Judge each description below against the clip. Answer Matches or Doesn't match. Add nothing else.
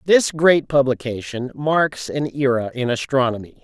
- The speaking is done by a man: Matches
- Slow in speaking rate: Matches